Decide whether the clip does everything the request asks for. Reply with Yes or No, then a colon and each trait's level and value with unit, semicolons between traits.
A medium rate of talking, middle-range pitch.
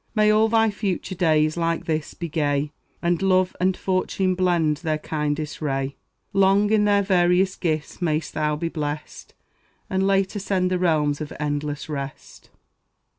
Yes: average, 155 wpm; medium, 170 Hz